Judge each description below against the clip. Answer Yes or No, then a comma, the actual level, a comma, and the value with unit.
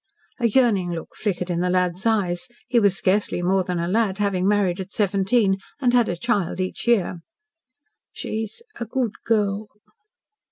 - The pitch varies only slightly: No, average, 3.5 semitones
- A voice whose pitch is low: No, high, 195 Hz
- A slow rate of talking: No, average, 165 wpm